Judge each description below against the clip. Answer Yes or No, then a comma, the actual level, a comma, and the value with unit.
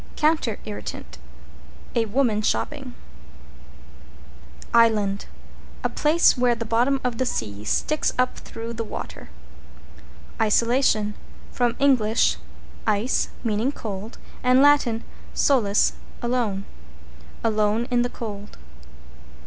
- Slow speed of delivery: Yes, slow, 100 wpm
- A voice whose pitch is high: Yes, high, 230 Hz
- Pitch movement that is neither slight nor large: Yes, average, 3.2 semitones